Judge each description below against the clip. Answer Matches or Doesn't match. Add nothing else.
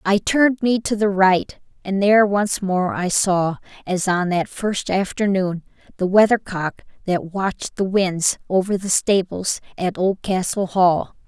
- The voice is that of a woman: Matches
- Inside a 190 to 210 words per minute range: Doesn't match